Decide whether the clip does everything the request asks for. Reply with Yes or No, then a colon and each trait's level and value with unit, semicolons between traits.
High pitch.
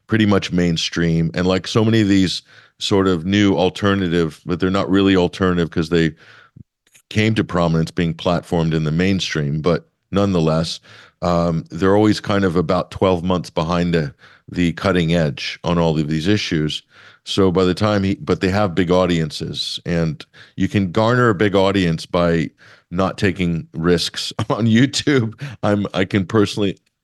No: very low, 95 Hz